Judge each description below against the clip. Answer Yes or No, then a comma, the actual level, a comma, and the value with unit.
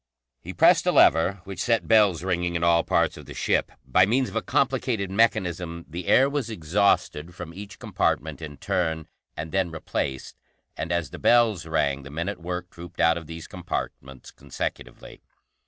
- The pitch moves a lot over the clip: No, average, 3.6 semitones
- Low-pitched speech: Yes, very low, 85 Hz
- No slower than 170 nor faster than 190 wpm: Yes, average, 180 wpm